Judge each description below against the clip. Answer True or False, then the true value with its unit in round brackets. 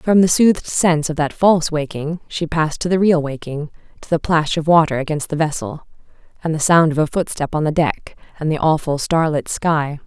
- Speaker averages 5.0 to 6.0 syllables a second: True (5.4 syllables/s)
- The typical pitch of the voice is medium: True (155 Hz)